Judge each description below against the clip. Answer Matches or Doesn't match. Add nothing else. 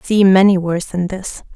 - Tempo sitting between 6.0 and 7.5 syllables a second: Doesn't match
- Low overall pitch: Doesn't match